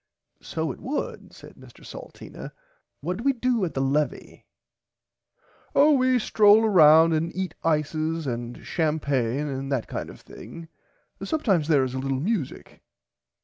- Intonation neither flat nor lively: No, wide, 7.0 semitones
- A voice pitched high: No, medium, 160 Hz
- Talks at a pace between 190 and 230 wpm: No, average, 150 wpm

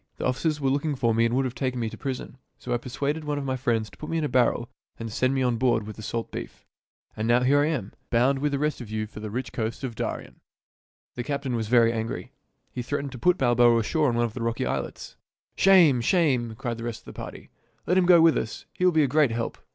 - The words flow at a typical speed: No, fast, 275 wpm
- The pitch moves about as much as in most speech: Yes, average, 3.7 semitones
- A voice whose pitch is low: Yes, low, 125 Hz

